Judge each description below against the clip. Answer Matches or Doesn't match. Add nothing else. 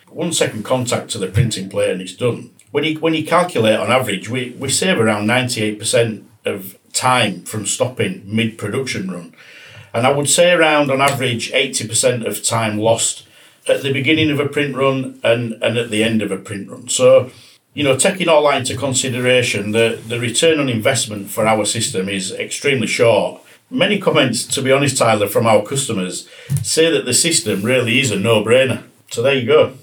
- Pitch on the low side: Matches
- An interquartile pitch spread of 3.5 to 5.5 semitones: Matches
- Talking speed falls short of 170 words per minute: Doesn't match